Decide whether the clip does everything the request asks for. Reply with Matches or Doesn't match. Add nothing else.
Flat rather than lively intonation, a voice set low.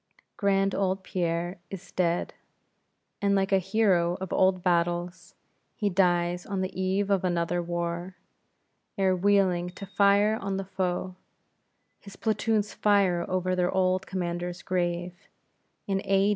Doesn't match